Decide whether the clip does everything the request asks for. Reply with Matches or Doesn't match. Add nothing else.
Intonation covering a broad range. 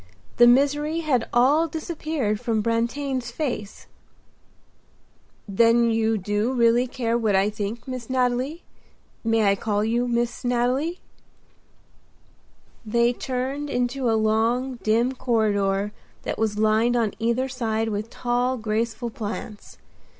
Doesn't match